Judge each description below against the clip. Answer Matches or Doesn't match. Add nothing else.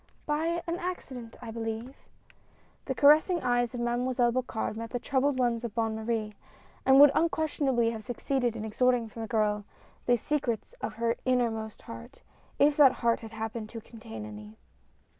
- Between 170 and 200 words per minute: Matches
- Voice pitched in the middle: Doesn't match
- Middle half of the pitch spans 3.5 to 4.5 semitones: Doesn't match